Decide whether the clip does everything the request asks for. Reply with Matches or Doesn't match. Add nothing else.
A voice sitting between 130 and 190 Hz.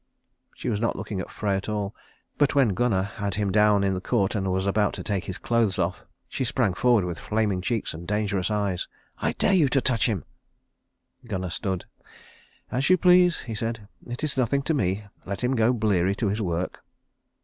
Doesn't match